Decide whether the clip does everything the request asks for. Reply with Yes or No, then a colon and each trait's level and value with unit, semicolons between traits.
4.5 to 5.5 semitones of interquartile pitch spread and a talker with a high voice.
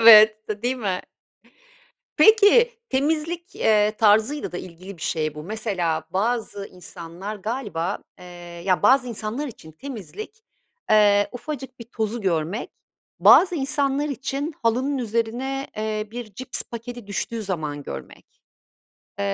Yes: average, 5.1 semitones; high, 220 Hz